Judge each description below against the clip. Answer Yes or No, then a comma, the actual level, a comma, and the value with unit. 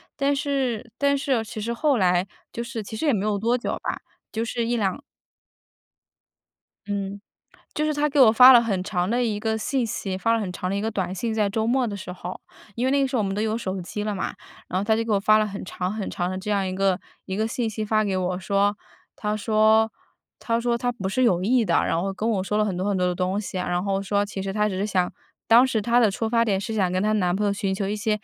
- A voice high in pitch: Yes, high, 210 Hz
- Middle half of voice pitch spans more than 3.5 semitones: No, average, 3.2 semitones